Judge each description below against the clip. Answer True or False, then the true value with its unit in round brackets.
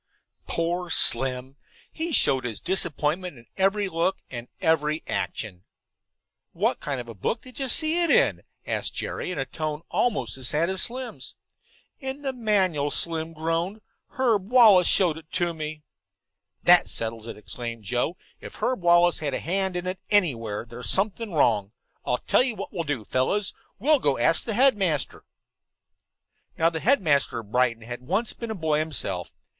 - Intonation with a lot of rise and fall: True (7.4 semitones)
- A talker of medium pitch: True (165 Hz)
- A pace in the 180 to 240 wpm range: False (170 wpm)